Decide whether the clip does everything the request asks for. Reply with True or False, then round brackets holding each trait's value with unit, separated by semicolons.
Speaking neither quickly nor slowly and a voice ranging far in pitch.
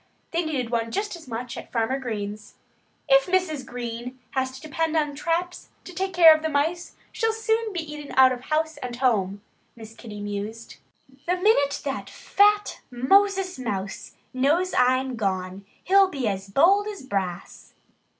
True (165 wpm; 7.3 semitones)